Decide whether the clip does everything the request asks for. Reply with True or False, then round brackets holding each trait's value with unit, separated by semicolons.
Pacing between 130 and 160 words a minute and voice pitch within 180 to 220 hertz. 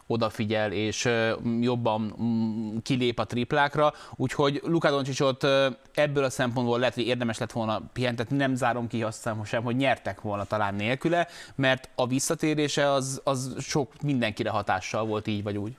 False (150 wpm; 120 Hz)